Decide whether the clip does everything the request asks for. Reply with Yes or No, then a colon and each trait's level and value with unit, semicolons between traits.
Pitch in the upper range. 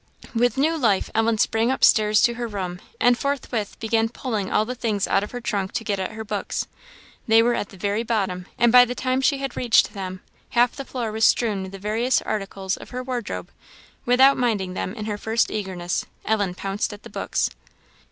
Yes: high, 220 Hz